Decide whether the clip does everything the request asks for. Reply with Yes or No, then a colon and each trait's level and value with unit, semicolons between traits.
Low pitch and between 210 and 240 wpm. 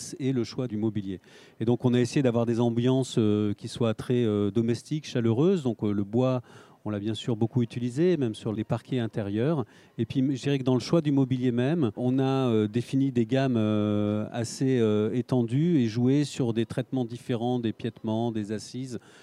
No: low, 120 Hz; average, 185 wpm